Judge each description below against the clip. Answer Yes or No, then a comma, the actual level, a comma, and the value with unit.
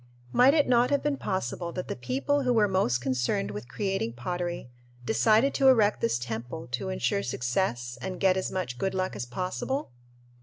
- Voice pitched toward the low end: No, medium, 175 Hz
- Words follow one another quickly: No, average, 185 wpm